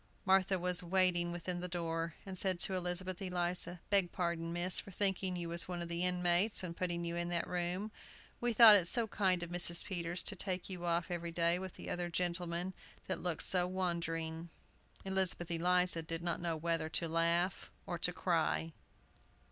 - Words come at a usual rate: Yes, average, 190 wpm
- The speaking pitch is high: No, medium, 175 Hz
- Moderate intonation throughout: No, narrow, 1.4 semitones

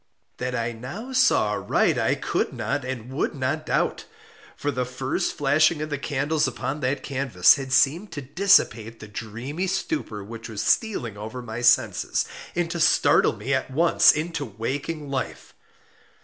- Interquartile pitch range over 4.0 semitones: Yes, average, 4.5 semitones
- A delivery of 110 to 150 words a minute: No, average, 165 wpm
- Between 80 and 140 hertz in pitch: Yes, low, 135 Hz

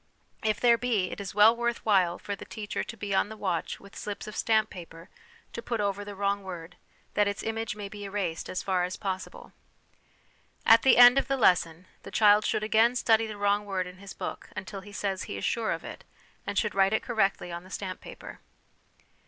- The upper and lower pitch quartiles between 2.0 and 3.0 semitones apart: Yes, narrow, 2.6 semitones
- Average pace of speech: No, fast, 220 wpm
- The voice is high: Yes, high, 205 Hz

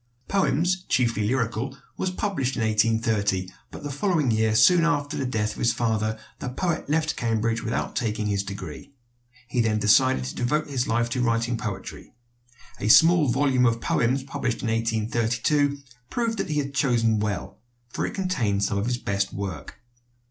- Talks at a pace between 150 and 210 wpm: Yes, average, 170 wpm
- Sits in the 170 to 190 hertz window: No, low, 120 Hz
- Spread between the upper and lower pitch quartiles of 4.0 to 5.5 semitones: Yes, average, 4.4 semitones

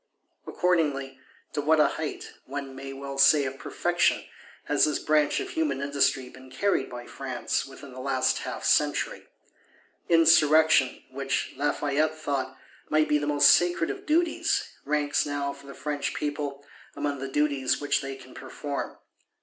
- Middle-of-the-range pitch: Yes, medium, 145 Hz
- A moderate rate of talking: Yes, average, 155 wpm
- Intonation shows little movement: Yes, narrow, 1.9 semitones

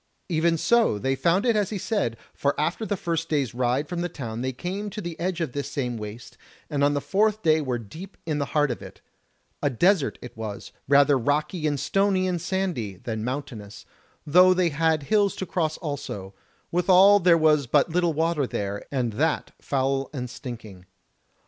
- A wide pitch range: Yes, wide, 5.8 semitones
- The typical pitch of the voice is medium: Yes, medium, 150 Hz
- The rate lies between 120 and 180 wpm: No, average, 195 wpm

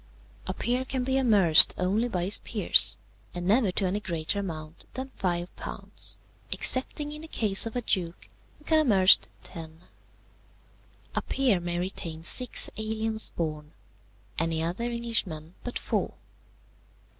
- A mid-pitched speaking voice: No, high, 195 Hz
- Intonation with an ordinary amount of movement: No, wide, 5.8 semitones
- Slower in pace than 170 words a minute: Yes, average, 145 wpm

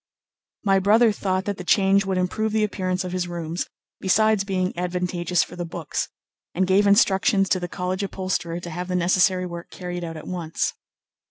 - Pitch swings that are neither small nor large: No, narrow, 1.7 semitones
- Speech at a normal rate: Yes, average, 185 wpm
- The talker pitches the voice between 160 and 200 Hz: Yes, medium, 185 Hz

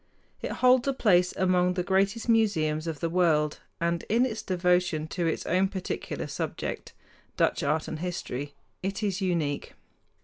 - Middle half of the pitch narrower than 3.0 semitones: No, average, 3.3 semitones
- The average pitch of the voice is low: No, medium, 180 Hz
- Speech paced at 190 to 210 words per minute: No, average, 160 wpm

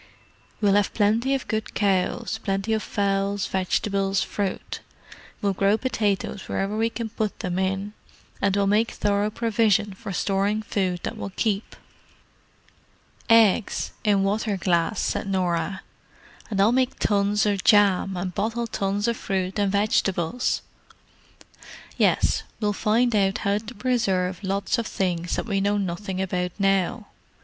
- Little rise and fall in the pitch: Yes, narrow, 2.0 semitones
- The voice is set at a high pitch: Yes, high, 200 Hz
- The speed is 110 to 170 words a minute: Yes, average, 140 wpm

